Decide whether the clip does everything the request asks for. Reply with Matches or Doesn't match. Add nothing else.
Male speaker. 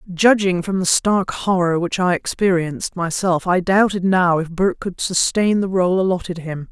Doesn't match